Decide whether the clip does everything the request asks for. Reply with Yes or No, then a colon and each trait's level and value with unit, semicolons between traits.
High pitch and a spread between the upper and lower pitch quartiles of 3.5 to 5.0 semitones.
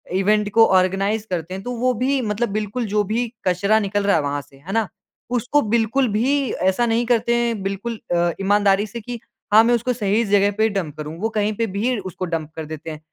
Yes: high, 210 Hz; average, 3.9 semitones